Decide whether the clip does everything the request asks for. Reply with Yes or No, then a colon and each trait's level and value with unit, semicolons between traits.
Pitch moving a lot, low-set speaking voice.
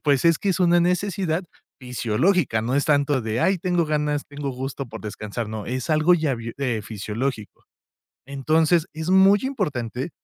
No: wide, 5.7 semitones; medium, 145 Hz